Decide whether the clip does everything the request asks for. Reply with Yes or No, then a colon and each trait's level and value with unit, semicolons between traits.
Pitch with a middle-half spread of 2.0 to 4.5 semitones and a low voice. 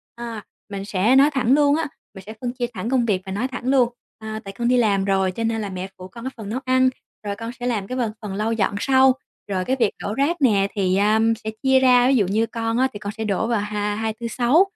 No: average, 3.8 semitones; high, 225 Hz